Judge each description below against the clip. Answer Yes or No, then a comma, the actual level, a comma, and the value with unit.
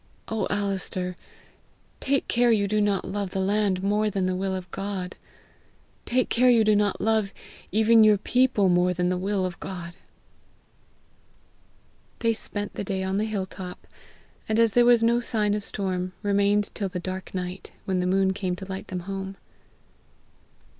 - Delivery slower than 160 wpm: No, average, 175 wpm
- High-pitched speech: Yes, high, 200 Hz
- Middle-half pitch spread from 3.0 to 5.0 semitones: No, narrow, 2.4 semitones